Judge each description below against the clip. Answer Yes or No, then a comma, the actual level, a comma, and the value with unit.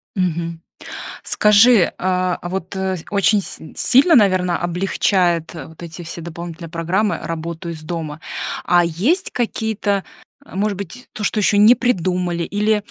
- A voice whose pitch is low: No, medium, 185 Hz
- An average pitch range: Yes, average, 3.5 semitones